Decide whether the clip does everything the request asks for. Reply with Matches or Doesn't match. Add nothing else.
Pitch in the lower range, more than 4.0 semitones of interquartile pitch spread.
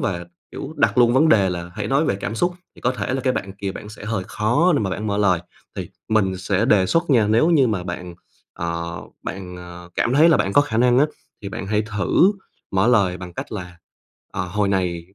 Matches